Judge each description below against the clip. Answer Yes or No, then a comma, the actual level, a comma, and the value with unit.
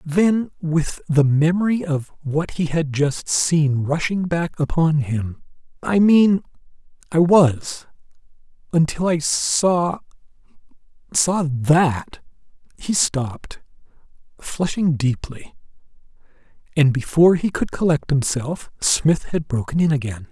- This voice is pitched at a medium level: Yes, medium, 155 Hz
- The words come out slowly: Yes, slow, 110 wpm